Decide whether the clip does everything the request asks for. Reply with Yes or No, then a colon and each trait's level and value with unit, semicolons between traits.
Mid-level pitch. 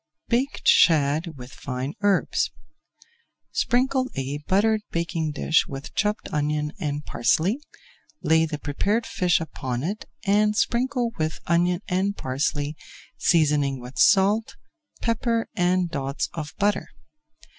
Yes: medium, 170 Hz